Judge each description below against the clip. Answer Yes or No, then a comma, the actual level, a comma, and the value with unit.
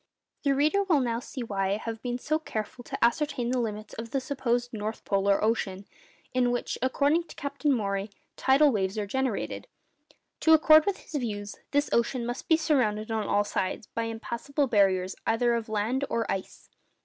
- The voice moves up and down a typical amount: Yes, average, 4.7 semitones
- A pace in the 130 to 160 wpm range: No, average, 185 wpm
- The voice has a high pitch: Yes, high, 235 Hz